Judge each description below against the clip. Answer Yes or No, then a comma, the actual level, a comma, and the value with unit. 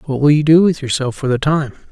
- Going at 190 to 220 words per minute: No, fast, 285 wpm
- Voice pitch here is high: No, medium, 145 Hz